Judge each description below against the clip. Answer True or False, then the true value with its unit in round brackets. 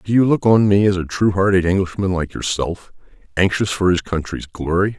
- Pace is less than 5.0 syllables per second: False (5.4 syllables/s)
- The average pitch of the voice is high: False (95 Hz)